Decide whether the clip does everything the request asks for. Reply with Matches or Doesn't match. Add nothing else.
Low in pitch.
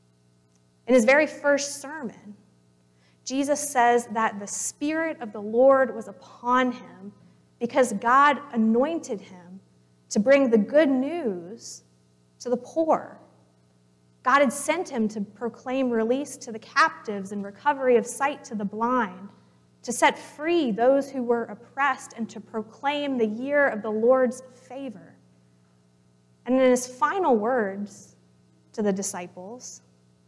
Doesn't match